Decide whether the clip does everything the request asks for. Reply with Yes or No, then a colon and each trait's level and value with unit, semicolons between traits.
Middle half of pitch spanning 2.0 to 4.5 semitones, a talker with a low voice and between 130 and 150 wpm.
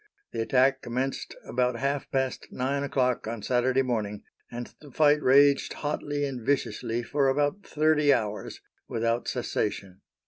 Yes: average, 3.1 semitones; low, 130 Hz; average, 140 wpm